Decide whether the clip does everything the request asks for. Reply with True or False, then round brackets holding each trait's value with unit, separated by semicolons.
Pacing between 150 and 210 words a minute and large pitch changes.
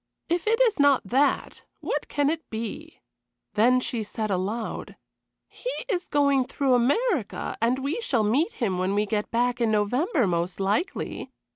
True (160 wpm; 5.8 semitones)